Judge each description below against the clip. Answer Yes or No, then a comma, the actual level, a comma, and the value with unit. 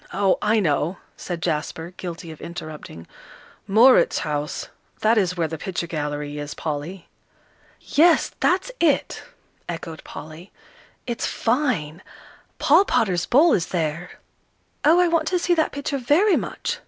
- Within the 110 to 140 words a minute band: Yes, slow, 135 wpm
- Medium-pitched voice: Yes, medium, 180 Hz